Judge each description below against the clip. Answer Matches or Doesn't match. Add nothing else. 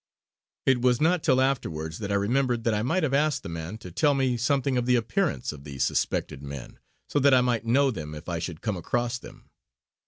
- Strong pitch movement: Matches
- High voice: Doesn't match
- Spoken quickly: Matches